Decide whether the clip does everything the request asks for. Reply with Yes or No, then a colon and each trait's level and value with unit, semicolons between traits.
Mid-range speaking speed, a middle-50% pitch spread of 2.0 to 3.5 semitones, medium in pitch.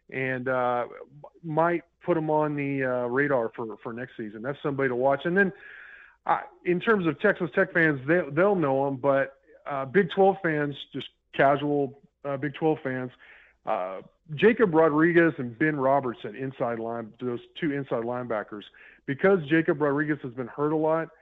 No: average, 175 wpm; average, 3.9 semitones; medium, 145 Hz